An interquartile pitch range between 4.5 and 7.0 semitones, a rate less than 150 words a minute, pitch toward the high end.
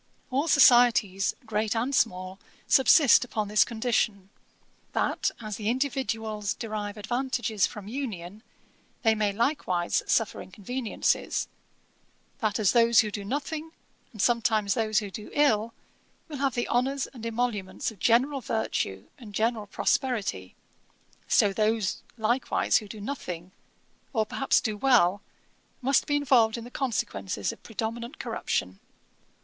No: average, 3.3 semitones; slow, 135 wpm; high, 225 Hz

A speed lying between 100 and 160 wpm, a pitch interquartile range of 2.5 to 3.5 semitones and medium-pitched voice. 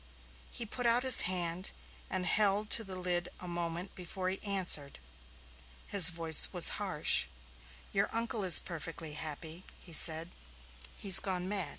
Yes: average, 150 wpm; average, 2.9 semitones; medium, 180 Hz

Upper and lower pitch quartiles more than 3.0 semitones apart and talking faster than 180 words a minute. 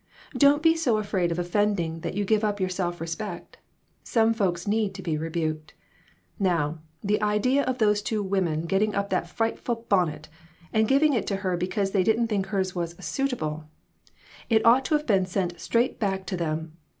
Yes: average, 4.2 semitones; average, 200 wpm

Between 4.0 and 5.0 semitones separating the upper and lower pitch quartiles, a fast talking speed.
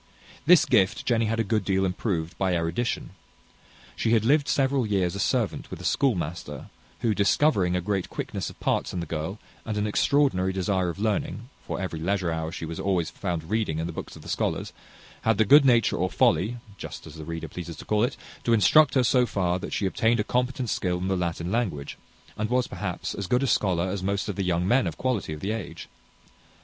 Yes: average, 4.7 semitones; fast, 220 wpm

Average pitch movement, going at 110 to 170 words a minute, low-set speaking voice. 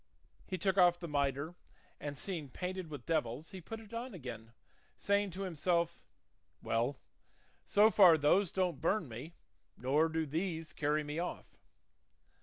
No: average, 4.4 semitones; average, 150 wpm; medium, 165 Hz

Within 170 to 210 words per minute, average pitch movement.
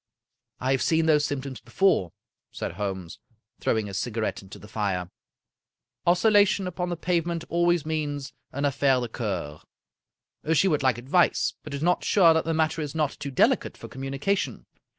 No: average, 175 wpm; wide, 6.1 semitones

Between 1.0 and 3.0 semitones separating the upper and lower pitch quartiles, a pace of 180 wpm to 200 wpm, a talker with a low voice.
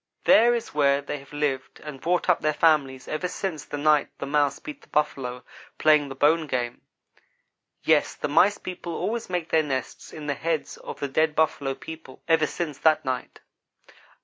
No: average, 2.7 semitones; average, 185 wpm; medium, 150 Hz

